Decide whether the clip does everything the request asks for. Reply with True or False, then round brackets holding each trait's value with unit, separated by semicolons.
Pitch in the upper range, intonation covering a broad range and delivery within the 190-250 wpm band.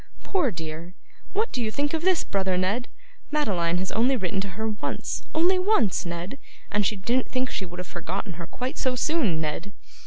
True (210 Hz; 6.5 semitones; 195 wpm)